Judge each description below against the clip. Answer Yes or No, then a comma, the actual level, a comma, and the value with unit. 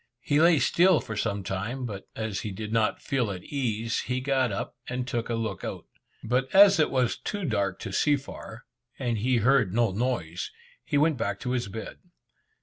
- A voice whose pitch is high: No, low, 120 Hz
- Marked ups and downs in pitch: No, average, 4.0 semitones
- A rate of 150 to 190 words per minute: No, average, 200 wpm